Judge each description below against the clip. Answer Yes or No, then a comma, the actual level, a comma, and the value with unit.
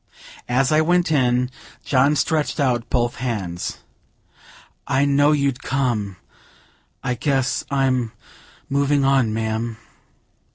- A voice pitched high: No, low, 130 Hz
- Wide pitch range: No, average, 2.9 semitones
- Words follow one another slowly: Yes, slow, 110 wpm